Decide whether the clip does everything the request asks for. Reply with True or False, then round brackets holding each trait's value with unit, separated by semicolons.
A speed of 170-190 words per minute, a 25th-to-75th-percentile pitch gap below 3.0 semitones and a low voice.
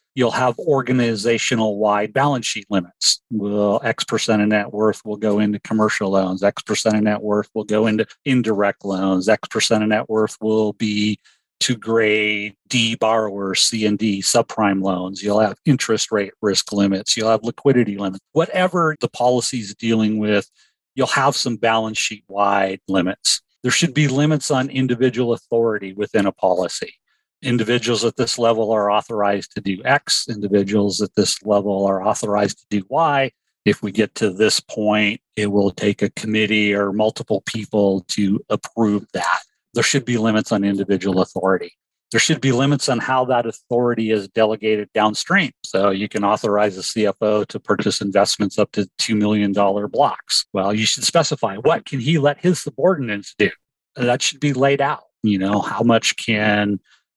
True (175 wpm; 2.5 semitones; 110 Hz)